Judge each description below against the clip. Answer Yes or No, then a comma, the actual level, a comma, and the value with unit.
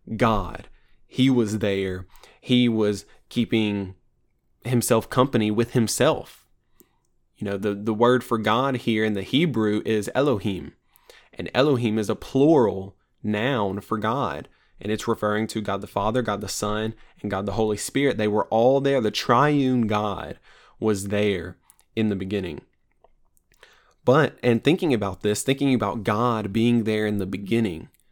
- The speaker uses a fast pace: No, average, 155 wpm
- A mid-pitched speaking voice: No, low, 110 Hz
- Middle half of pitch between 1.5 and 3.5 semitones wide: Yes, average, 3.0 semitones